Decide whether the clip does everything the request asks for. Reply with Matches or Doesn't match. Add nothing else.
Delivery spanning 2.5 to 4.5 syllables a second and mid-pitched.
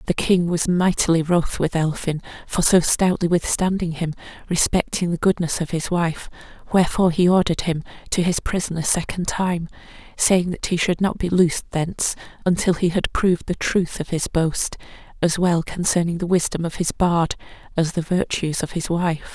Doesn't match